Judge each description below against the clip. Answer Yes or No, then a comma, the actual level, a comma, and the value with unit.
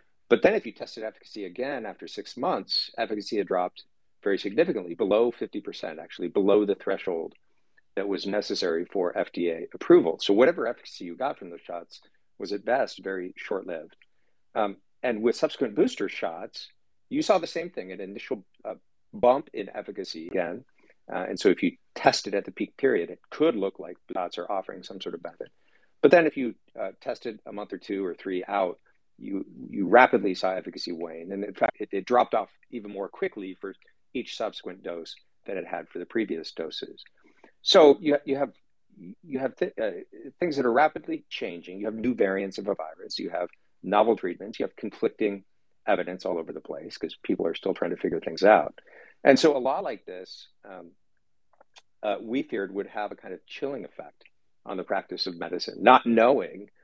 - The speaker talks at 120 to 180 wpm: No, average, 195 wpm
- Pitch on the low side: Yes, low, 110 Hz